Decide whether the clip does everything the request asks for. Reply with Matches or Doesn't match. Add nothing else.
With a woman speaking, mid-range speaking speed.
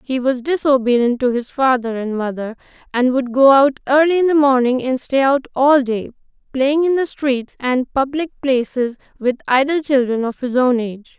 Matches